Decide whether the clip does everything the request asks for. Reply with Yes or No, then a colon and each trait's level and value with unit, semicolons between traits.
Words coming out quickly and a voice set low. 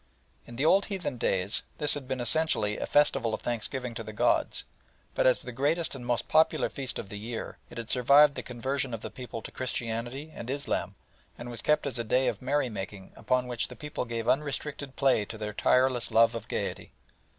Yes: fast, 210 wpm; low, 125 Hz